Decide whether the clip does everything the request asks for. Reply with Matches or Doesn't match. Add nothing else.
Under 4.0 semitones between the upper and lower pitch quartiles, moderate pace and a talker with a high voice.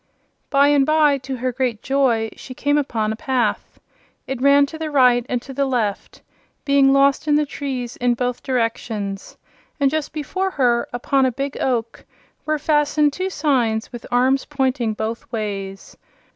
Matches